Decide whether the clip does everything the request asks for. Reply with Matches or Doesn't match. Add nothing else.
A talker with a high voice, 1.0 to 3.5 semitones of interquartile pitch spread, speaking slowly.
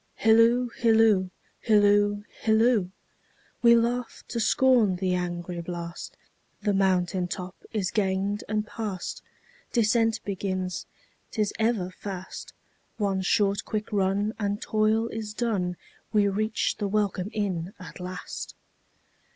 Matches